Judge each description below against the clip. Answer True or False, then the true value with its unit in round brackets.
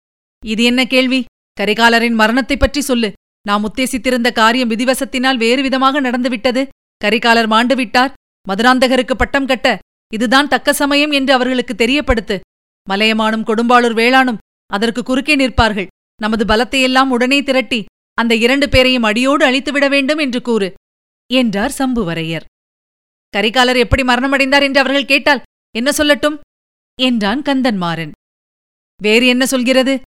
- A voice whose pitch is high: True (255 Hz)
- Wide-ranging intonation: False (2.8 semitones)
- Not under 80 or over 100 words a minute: False (115 wpm)